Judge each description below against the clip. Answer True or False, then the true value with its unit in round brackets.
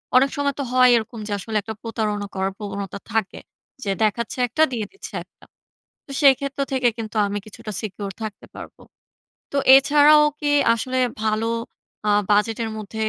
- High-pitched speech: True (225 Hz)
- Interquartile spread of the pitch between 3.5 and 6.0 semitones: True (3.9 semitones)